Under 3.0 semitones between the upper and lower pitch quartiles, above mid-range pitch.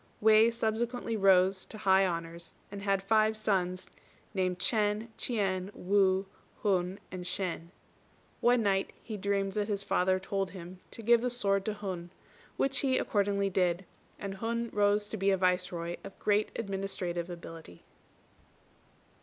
Yes: narrow, 2.6 semitones; high, 195 Hz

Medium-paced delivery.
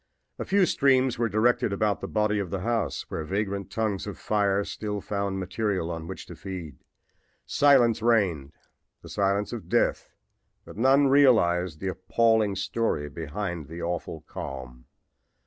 Yes: average, 150 wpm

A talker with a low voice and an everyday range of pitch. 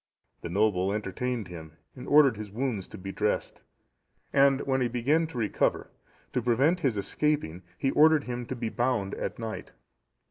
Yes: low, 120 Hz; average, 4.8 semitones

